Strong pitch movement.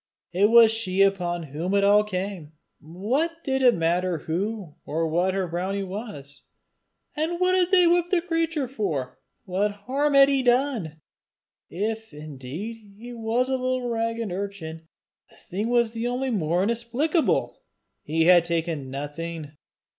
Yes: wide, 6.5 semitones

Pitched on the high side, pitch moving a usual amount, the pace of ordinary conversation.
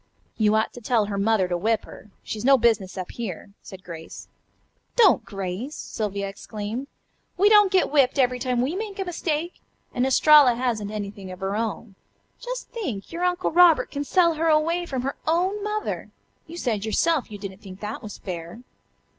No: high, 245 Hz; wide, 8.4 semitones; average, 190 wpm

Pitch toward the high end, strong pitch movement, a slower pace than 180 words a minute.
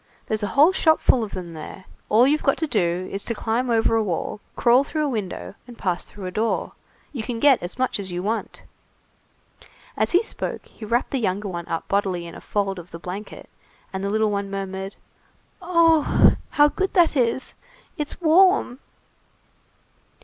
No: high, 220 Hz; wide, 6.3 semitones; average, 185 wpm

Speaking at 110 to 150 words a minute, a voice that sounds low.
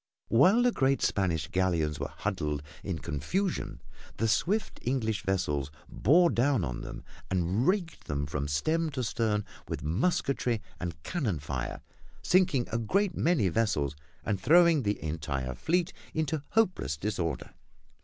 Yes: average, 140 wpm; low, 105 Hz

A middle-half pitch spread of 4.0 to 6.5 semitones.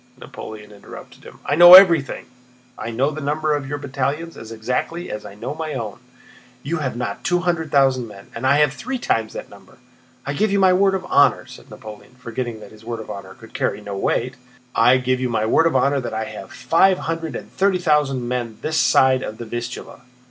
Yes: average, 5.3 semitones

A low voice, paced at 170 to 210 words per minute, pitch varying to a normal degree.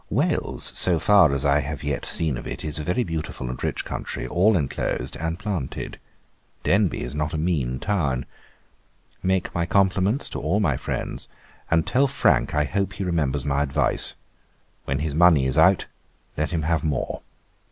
Yes: very low, 80 Hz; average, 175 wpm; average, 4.6 semitones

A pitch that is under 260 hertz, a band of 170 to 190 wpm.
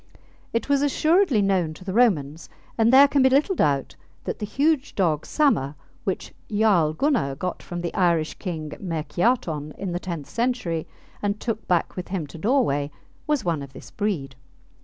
Yes: high, 190 Hz; average, 175 wpm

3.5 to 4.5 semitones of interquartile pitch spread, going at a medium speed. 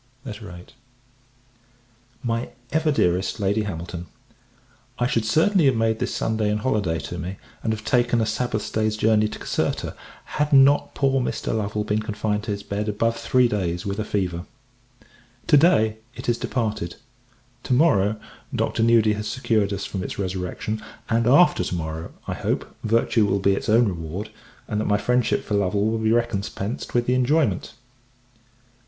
No: average, 2.9 semitones; average, 170 wpm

